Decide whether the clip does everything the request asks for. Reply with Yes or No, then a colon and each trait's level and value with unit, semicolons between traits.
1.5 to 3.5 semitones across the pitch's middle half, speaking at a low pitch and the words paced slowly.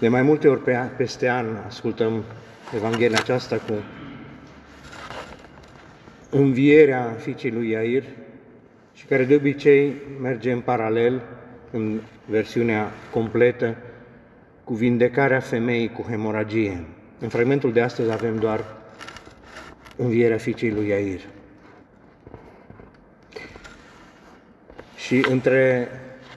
Yes: narrow, 2.6 semitones; low, 120 Hz; slow, 95 wpm